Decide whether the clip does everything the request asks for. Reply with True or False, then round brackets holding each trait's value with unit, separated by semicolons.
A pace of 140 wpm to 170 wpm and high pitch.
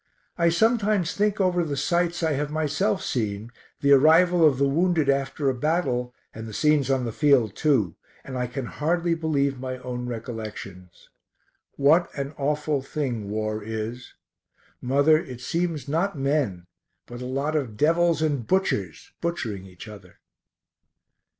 False (150 wpm; 140 Hz)